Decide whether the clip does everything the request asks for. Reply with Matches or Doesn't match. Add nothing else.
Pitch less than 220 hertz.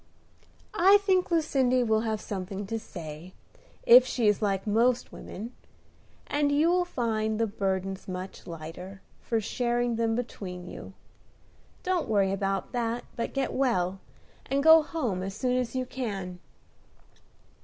Doesn't match